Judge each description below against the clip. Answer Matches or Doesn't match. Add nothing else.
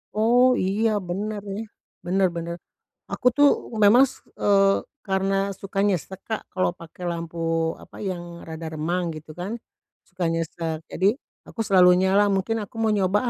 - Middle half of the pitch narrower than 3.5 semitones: Matches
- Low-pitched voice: Doesn't match